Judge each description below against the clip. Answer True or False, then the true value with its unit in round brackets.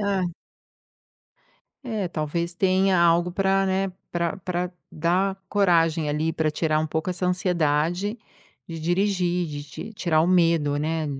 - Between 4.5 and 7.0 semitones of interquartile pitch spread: False (3.0 semitones)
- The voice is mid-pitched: True (175 Hz)